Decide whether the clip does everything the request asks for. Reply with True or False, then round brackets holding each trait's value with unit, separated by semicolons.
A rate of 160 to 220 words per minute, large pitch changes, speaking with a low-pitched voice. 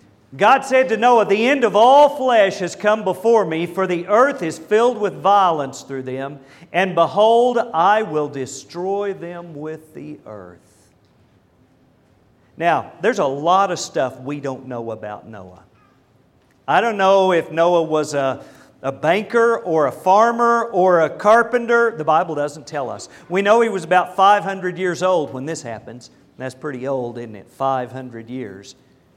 False (165 wpm; 7.4 semitones; 170 Hz)